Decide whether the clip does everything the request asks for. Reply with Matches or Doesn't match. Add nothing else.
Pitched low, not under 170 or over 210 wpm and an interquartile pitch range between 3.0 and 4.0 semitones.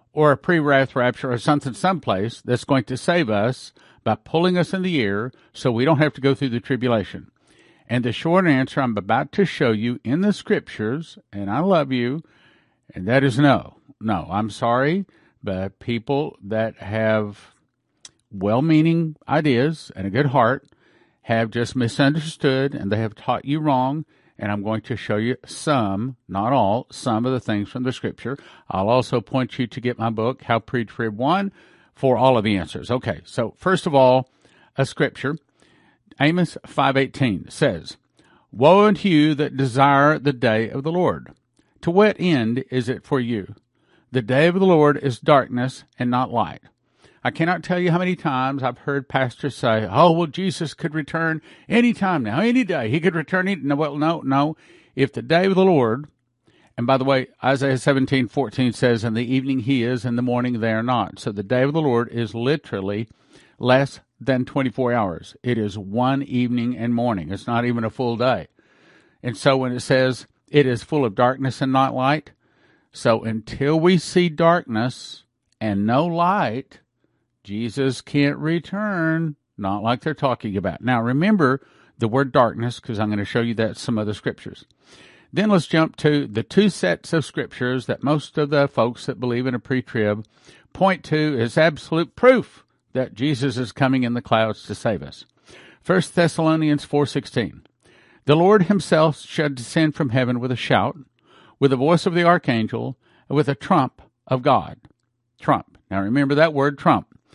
Doesn't match